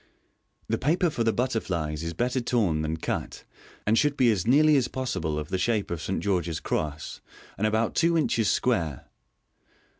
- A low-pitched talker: Yes, low, 110 Hz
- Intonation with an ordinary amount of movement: No, wide, 7.3 semitones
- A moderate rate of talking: Yes, average, 180 wpm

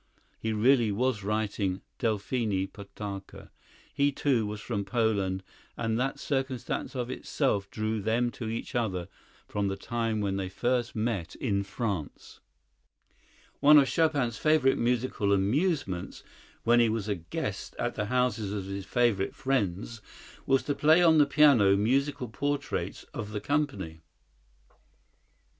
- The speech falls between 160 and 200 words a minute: No, average, 140 wpm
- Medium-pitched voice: No, low, 110 Hz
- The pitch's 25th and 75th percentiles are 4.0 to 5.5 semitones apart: Yes, average, 4.4 semitones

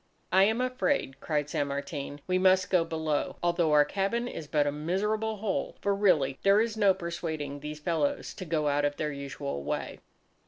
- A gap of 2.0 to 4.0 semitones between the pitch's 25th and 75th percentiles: No, average, 5.1 semitones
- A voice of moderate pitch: Yes, medium, 165 Hz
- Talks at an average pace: Yes, average, 190 wpm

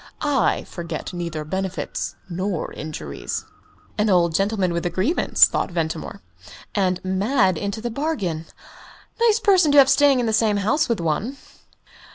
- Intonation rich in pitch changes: Yes, wide, 5.8 semitones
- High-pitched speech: Yes, high, 195 Hz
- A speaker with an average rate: Yes, average, 150 wpm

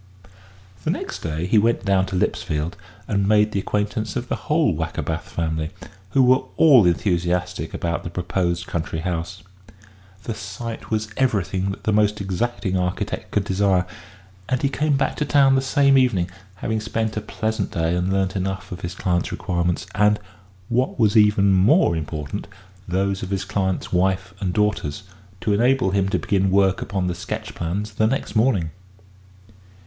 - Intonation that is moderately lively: Yes, average, 3.3 semitones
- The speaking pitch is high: No, very low, 95 Hz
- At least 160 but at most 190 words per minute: Yes, average, 170 wpm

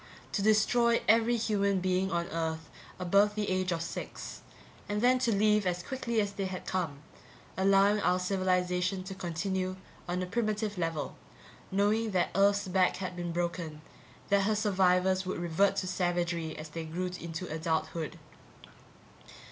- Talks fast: No, average, 155 wpm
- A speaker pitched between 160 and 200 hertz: Yes, medium, 185 Hz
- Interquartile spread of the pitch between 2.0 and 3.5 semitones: Yes, narrow, 2.6 semitones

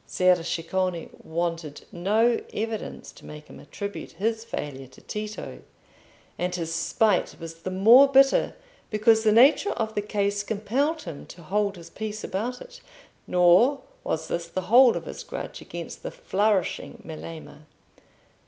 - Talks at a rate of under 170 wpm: Yes, average, 150 wpm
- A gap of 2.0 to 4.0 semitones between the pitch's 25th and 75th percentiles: No, average, 4.7 semitones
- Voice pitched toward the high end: Yes, high, 200 Hz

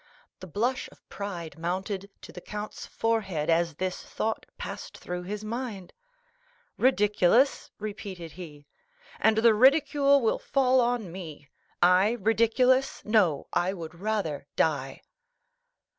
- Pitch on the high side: Yes, high, 205 Hz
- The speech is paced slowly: Yes, slow, 125 wpm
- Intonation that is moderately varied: Yes, average, 4.8 semitones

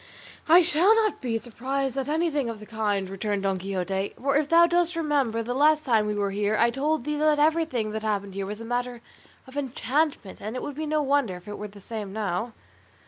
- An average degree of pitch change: No, wide, 6.1 semitones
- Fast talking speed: Yes, fast, 225 wpm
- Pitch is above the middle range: Yes, high, 245 Hz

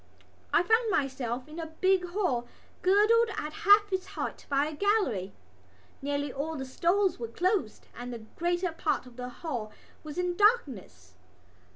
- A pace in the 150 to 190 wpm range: Yes, average, 160 wpm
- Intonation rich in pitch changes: Yes, wide, 7.1 semitones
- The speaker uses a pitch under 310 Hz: No, very high, 320 Hz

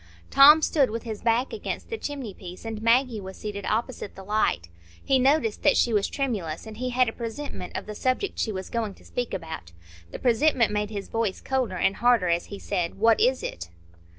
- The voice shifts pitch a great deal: No, average, 4.2 semitones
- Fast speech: Yes, fast, 210 wpm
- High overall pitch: Yes, high, 225 Hz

